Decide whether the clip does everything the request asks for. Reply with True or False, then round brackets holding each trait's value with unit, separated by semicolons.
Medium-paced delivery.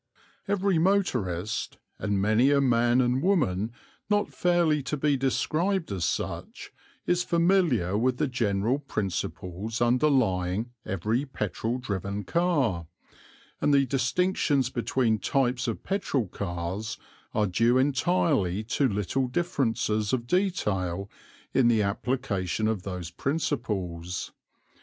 False (115 wpm)